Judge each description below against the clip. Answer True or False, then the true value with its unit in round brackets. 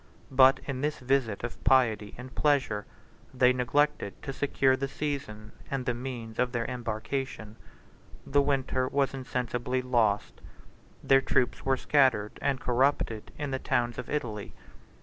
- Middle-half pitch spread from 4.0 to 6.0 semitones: False (2.5 semitones)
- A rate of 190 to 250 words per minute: False (150 wpm)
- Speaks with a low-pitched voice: True (130 Hz)